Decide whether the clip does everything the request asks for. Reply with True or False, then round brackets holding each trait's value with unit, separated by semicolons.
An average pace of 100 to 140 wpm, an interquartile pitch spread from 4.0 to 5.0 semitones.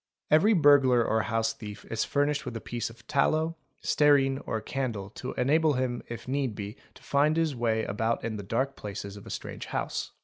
False (200 wpm; 4.3 semitones)